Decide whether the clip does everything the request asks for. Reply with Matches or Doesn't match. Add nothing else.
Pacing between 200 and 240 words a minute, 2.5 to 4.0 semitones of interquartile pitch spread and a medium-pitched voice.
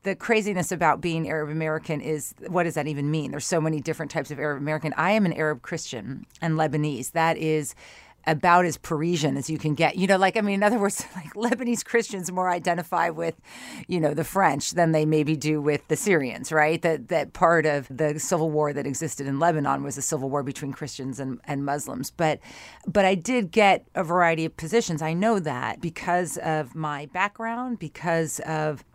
Matches